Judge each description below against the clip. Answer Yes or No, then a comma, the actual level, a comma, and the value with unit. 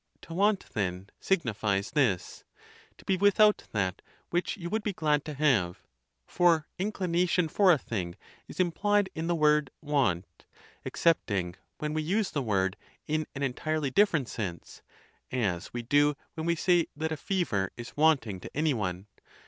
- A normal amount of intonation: No, wide, 8.4 semitones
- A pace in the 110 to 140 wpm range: No, average, 155 wpm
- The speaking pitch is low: No, medium, 150 Hz